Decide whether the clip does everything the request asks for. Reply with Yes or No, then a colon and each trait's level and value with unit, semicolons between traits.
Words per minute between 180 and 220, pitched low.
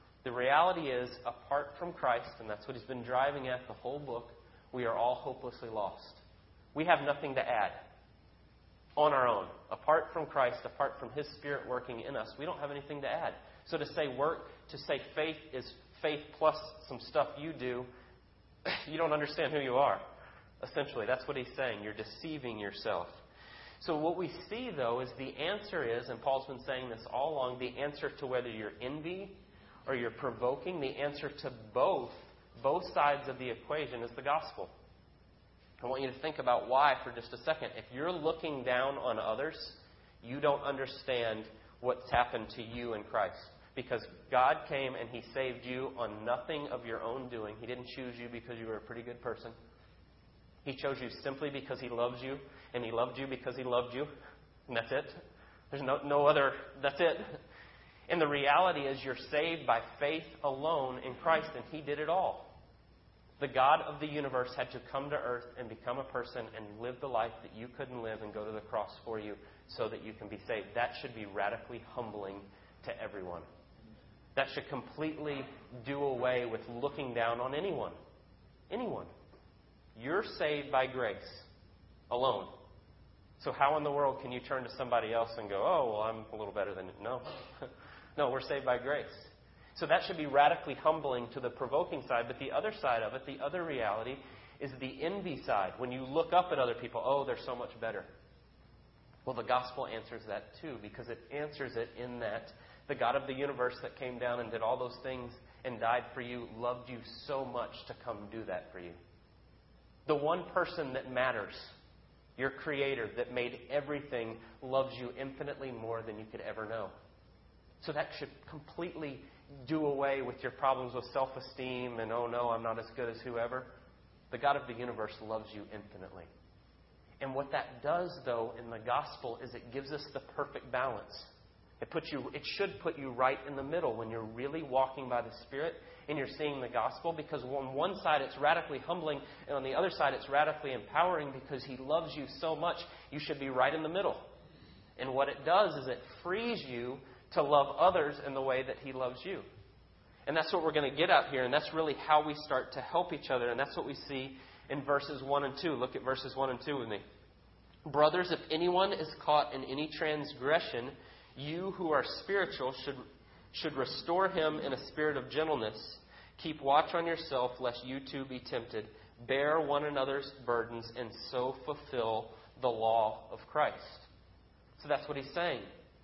Yes: average, 195 wpm; low, 130 Hz